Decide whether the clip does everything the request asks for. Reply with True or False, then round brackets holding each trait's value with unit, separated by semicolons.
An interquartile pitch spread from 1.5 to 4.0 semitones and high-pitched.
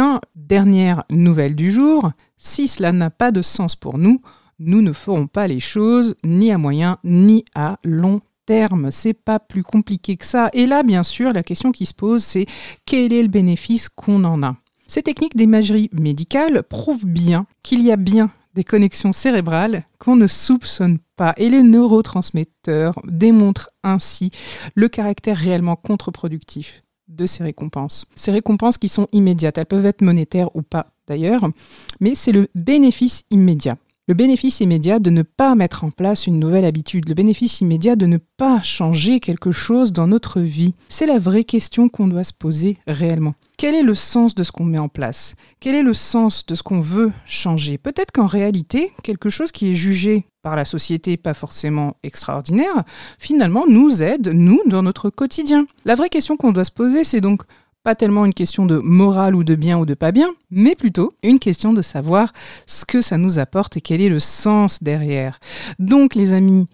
False (5.2 semitones; 195 Hz)